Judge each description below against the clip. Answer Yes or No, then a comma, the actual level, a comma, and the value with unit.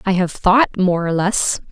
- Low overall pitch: No, high, 190 Hz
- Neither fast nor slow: No, fast, 210 wpm